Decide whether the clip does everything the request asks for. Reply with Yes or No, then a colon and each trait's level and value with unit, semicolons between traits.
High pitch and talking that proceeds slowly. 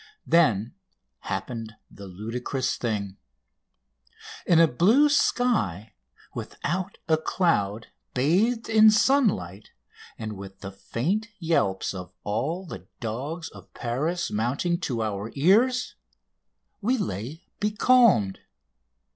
No: medium, 140 Hz; slow, 105 wpm